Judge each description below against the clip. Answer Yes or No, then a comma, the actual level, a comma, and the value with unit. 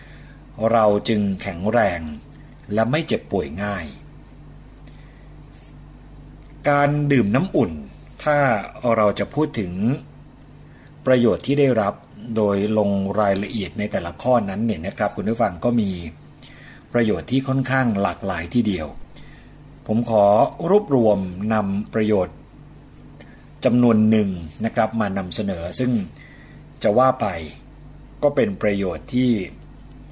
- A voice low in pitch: Yes, low, 110 Hz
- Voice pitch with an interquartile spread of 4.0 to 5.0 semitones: Yes, average, 4.7 semitones